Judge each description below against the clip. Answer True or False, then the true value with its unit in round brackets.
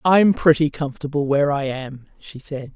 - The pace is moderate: True (195 wpm)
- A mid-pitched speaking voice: True (145 Hz)